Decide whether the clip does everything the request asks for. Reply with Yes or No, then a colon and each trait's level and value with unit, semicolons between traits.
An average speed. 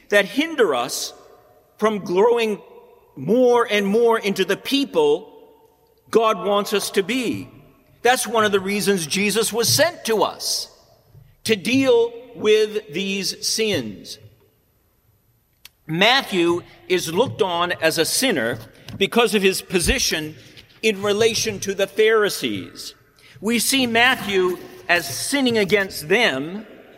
No: slow, 120 wpm